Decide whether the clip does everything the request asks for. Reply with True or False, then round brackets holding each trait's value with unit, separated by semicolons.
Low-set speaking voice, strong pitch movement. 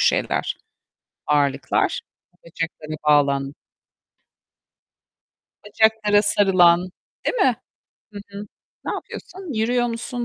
False (205 Hz; 6.9 semitones)